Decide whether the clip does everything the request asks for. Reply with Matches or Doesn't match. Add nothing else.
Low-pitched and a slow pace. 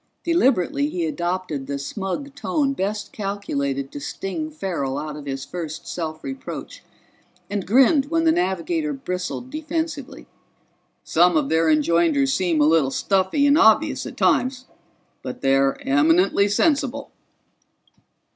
Doesn't match